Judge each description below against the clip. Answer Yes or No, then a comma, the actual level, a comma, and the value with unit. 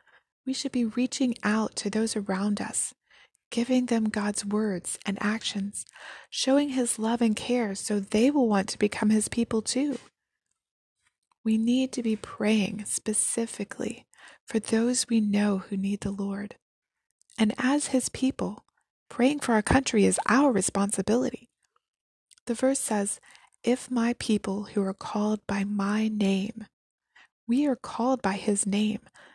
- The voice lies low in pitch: No, high, 220 Hz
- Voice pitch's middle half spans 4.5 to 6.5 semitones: No, average, 3.4 semitones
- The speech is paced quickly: No, average, 145 wpm